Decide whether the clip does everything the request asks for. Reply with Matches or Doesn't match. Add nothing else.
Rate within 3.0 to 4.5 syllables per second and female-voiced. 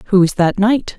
Matches